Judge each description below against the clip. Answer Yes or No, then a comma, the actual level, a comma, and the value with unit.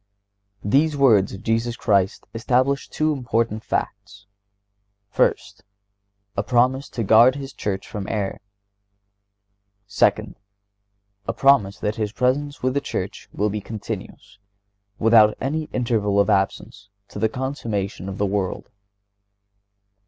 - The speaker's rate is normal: No, slow, 115 wpm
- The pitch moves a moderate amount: Yes, average, 4.0 semitones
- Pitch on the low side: Yes, low, 105 Hz